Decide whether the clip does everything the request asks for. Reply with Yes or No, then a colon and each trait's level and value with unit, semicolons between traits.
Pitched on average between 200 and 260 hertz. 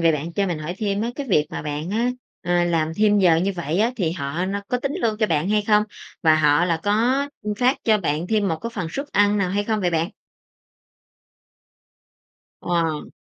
No: medium, 185 Hz